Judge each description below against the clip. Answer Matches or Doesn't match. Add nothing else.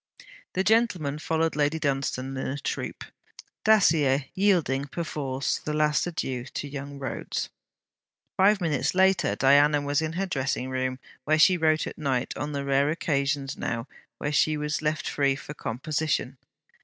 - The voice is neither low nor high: Matches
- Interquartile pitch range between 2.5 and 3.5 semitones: Matches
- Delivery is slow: Doesn't match